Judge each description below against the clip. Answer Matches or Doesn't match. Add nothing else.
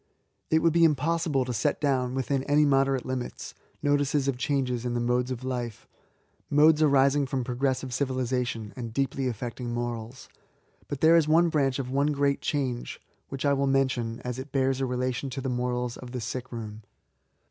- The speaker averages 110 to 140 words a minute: Doesn't match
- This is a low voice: Matches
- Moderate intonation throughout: Doesn't match